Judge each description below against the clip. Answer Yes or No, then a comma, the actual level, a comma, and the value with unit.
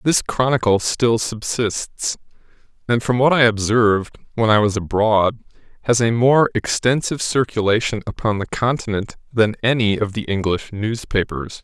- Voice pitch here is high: No, low, 115 Hz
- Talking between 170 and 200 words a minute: No, average, 140 wpm